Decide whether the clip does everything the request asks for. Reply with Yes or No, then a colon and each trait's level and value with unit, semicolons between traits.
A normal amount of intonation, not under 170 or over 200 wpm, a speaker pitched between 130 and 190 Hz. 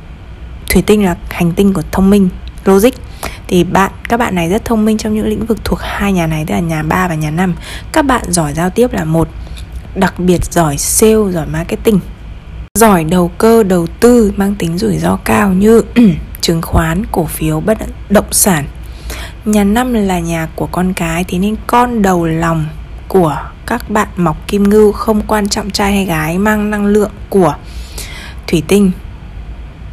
Yes: average, 4.6 semitones; average, 185 wpm; medium, 185 Hz